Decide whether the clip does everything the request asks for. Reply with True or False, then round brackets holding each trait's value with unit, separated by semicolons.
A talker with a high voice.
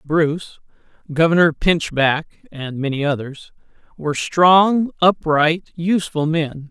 False (160 Hz)